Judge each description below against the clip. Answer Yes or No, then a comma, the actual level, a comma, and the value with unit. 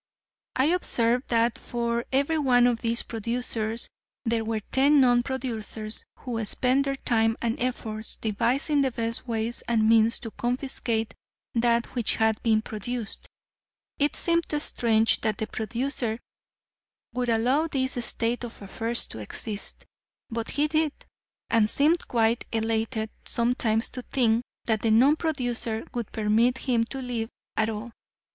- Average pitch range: No, narrow, 2.3 semitones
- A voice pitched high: Yes, high, 235 Hz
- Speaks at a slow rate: No, average, 145 wpm